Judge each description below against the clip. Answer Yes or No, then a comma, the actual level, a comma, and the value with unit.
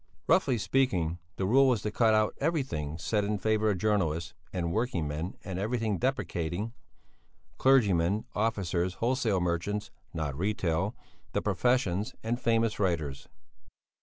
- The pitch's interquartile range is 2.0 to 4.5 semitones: No, average, 4.9 semitones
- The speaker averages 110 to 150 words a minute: Yes, slow, 135 wpm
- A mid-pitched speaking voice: No, low, 105 Hz